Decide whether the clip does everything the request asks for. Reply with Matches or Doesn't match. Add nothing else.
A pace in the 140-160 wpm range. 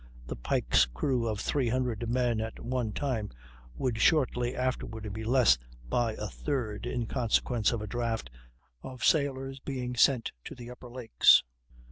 Matches